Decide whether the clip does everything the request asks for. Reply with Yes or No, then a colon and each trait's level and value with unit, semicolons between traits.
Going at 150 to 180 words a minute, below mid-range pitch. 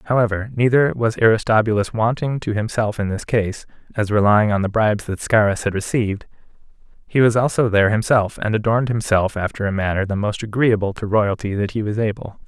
No: average, 190 wpm; low, 110 Hz